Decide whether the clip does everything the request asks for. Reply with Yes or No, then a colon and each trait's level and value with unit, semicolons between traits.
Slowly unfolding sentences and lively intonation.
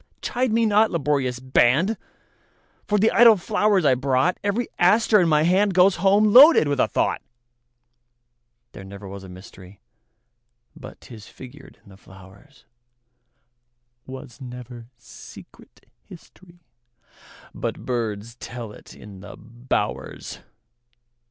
Yes: slow, 100 wpm; wide, 6.8 semitones